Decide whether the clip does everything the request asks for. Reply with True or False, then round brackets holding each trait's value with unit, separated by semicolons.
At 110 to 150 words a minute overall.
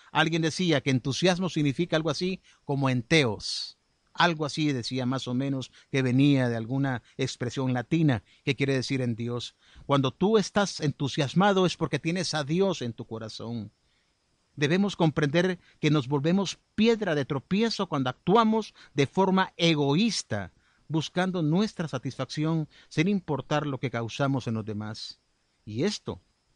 True (145 wpm)